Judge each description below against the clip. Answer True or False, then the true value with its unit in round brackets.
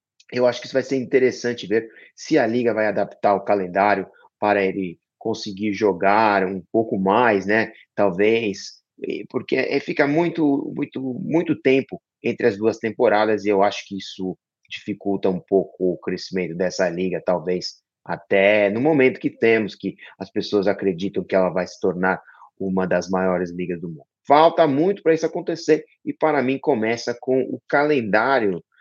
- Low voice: True (105 Hz)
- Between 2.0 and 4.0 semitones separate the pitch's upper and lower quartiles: False (5.2 semitones)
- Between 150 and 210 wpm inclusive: True (165 wpm)